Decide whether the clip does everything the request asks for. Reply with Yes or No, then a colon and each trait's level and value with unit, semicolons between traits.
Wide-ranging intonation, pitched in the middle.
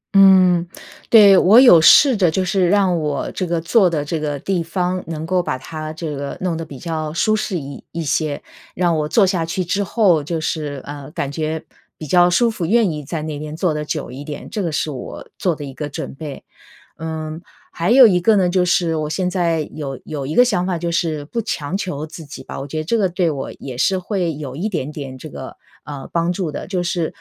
No: average, 3.4 semitones; medium, 165 Hz